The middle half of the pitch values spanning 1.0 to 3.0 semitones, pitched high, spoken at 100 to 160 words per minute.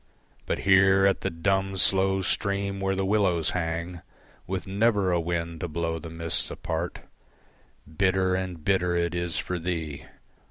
No: narrow, 2.5 semitones; very low, 90 Hz; average, 155 wpm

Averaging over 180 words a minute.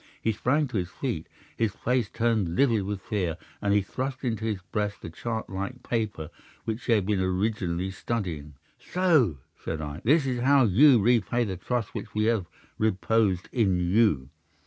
No: average, 175 wpm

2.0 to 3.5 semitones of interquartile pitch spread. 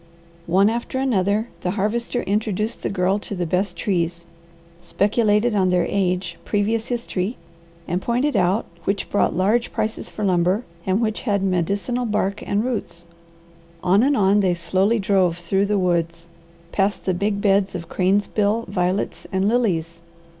Yes: average, 2.9 semitones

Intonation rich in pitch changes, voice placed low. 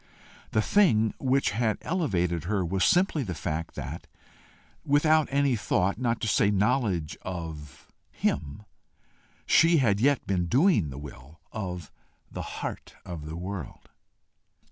Yes: wide, 7.7 semitones; low, 100 Hz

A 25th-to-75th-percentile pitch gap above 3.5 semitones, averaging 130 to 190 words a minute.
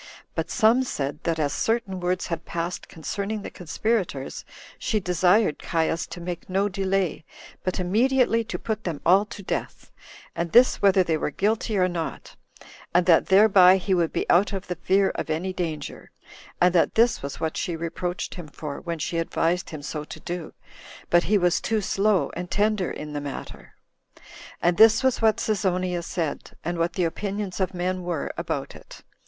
No: average, 3.2 semitones; average, 180 wpm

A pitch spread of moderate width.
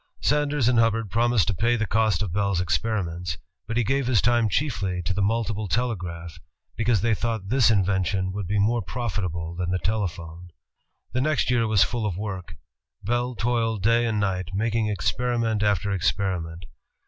Yes: average, 4.1 semitones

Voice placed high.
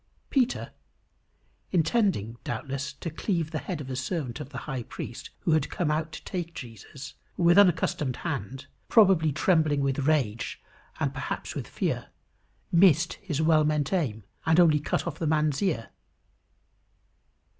No: medium, 155 Hz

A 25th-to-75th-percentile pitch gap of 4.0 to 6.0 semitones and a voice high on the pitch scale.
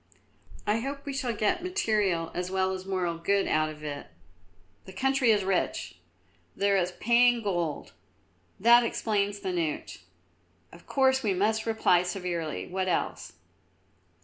Yes: average, 4.3 semitones; high, 195 Hz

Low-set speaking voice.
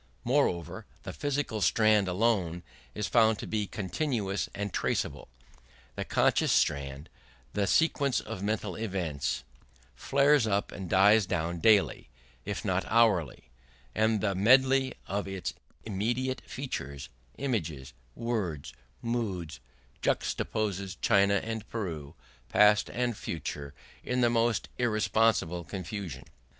Yes: low, 105 Hz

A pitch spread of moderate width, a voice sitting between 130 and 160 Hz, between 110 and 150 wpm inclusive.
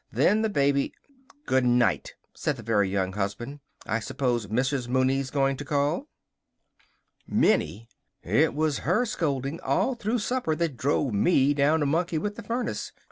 No: average, 5.0 semitones; medium, 140 Hz; average, 160 wpm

